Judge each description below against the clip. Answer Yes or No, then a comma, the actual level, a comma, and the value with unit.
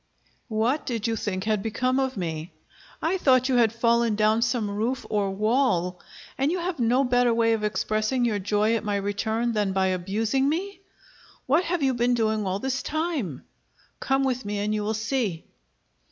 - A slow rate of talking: No, average, 185 wpm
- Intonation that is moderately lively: Yes, average, 3.8 semitones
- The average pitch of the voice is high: Yes, high, 225 Hz